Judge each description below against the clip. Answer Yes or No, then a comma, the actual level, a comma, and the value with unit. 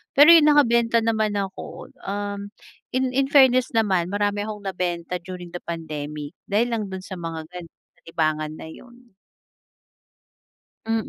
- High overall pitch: Yes, high, 200 Hz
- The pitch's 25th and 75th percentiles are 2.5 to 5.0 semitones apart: No, wide, 5.5 semitones